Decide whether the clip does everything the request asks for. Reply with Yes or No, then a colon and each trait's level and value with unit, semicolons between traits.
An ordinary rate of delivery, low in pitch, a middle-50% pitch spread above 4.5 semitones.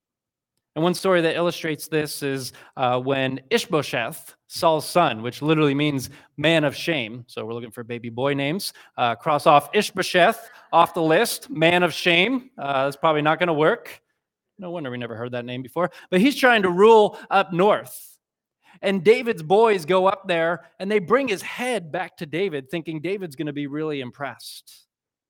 No: average, 180 wpm; medium, 165 Hz; average, 5.1 semitones